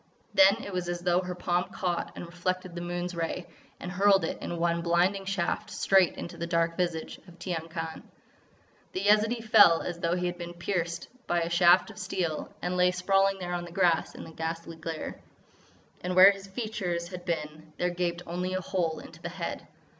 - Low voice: No, medium, 175 Hz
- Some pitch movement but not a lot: No, narrow, 1.7 semitones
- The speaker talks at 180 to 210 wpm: Yes, average, 200 wpm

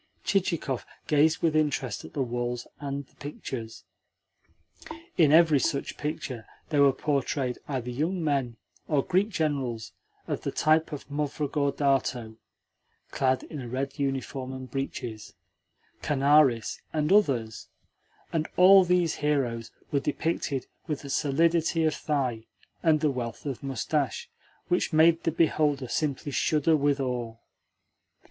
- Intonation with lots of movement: No, average, 3.2 semitones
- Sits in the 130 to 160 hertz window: Yes, medium, 140 Hz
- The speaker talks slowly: Yes, slow, 130 wpm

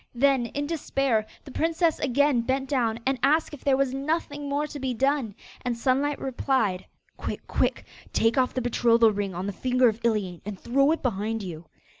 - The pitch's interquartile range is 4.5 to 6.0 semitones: No, average, 3.9 semitones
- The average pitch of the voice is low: No, very high, 255 Hz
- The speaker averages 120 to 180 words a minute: No, average, 190 wpm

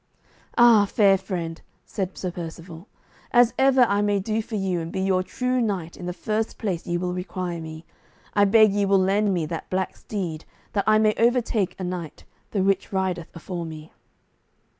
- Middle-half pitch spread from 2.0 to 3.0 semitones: No, average, 3.5 semitones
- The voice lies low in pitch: No, high, 190 Hz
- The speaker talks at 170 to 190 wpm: Yes, average, 185 wpm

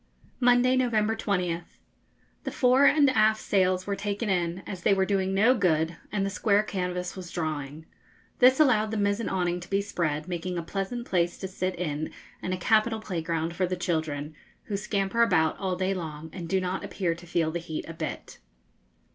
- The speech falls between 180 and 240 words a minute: Yes, average, 190 wpm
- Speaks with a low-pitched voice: No, medium, 185 Hz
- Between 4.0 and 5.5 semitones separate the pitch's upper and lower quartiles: No, average, 3.6 semitones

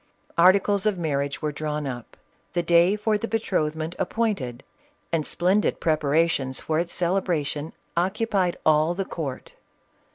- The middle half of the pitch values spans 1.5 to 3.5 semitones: No, average, 4.1 semitones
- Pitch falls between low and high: Yes, medium, 170 Hz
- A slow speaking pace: Yes, slow, 130 wpm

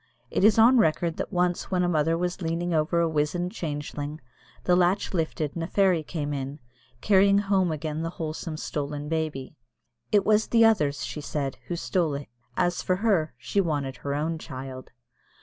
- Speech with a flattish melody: No, average, 3.5 semitones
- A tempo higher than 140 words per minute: Yes, average, 185 wpm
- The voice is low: No, medium, 165 Hz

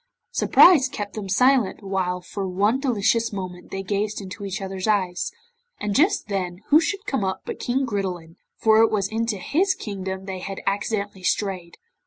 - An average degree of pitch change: Yes, average, 3.1 semitones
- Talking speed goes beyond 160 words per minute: Yes, average, 175 wpm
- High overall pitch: Yes, high, 200 Hz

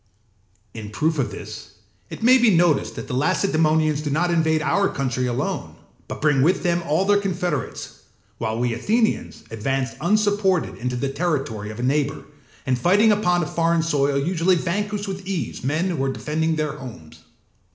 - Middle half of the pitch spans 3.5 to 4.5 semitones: No, average, 5.3 semitones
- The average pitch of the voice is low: No, medium, 155 Hz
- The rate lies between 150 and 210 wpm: Yes, average, 170 wpm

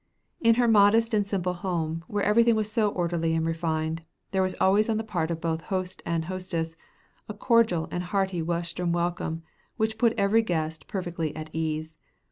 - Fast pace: No, average, 180 wpm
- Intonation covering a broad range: No, average, 4.2 semitones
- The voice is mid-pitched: Yes, medium, 180 Hz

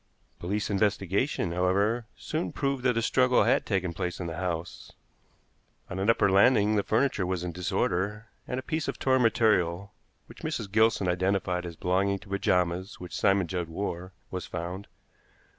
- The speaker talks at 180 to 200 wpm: No, average, 165 wpm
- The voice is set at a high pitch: No, very low, 95 Hz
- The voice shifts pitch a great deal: No, average, 3.5 semitones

